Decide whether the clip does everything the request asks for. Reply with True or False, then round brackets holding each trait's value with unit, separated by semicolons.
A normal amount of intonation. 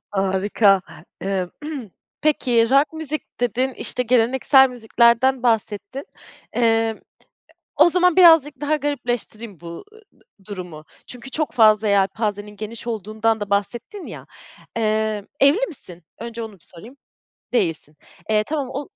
True (4.4 semitones)